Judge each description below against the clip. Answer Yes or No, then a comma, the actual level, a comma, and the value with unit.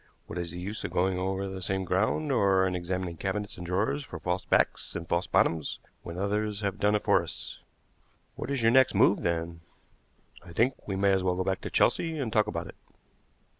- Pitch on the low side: Yes, very low, 95 Hz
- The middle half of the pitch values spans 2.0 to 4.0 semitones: Yes, average, 3.0 semitones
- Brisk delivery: Yes, fast, 215 wpm